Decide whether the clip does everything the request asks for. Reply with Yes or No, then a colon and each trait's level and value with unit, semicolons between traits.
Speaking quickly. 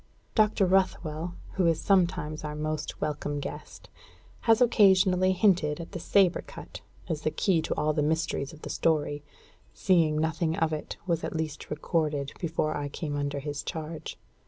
No: average, 165 wpm